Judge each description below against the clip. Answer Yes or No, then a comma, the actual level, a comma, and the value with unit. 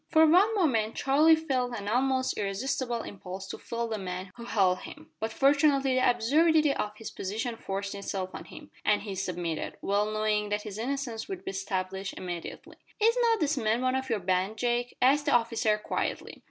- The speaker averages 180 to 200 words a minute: Yes, average, 190 wpm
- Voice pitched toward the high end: Yes, high, 230 Hz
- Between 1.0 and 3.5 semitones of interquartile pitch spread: No, average, 5.3 semitones